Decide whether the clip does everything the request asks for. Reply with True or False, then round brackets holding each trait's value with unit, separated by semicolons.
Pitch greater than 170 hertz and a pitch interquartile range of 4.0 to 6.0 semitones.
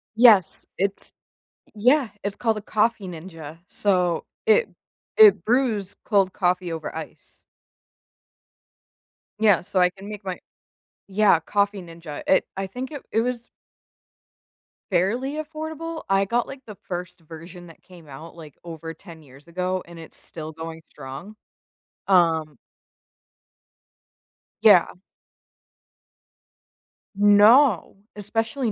True (190 Hz; 5.0 semitones)